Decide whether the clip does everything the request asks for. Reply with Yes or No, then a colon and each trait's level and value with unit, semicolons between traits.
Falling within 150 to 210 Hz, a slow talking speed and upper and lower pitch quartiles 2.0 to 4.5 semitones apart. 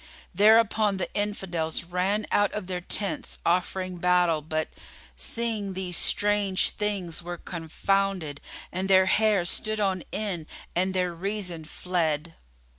Yes: medium, 185 Hz; slow, 125 wpm; average, 2.9 semitones